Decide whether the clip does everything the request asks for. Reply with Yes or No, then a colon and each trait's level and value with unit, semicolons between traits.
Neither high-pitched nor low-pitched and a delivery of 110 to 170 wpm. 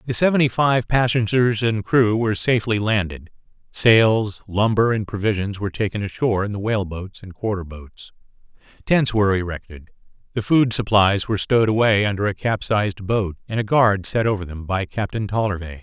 No: low, 105 Hz; average, 165 wpm